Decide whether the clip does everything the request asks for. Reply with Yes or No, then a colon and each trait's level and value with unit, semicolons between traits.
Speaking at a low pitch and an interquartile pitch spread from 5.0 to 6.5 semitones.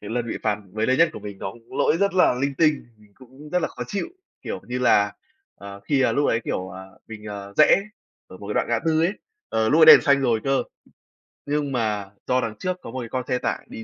Yes: low, 125 Hz; wide, 5.4 semitones